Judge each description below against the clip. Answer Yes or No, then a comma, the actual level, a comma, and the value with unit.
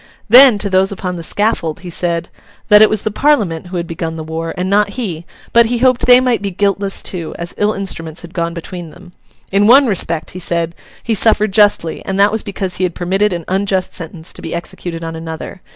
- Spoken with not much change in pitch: No, average, 3.6 semitones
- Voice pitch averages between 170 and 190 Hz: Yes, medium, 185 Hz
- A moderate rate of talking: No, fast, 225 wpm